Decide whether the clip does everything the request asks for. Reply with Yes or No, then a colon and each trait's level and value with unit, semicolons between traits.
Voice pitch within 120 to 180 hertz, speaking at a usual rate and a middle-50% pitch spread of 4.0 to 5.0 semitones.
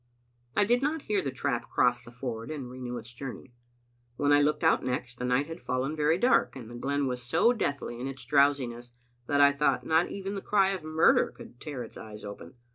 No: medium, 140 Hz; fast, 220 wpm; average, 4.4 semitones